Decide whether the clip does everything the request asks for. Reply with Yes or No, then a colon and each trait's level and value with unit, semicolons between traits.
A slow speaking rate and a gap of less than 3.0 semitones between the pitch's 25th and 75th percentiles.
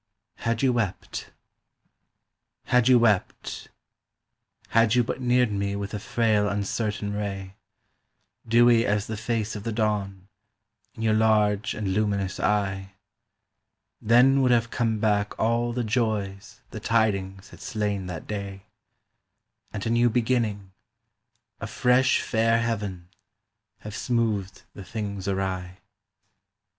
Yes: slow, 125 wpm; narrow, 2.6 semitones